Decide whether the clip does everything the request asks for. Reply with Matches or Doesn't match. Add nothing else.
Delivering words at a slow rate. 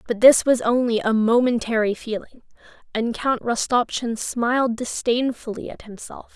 Matches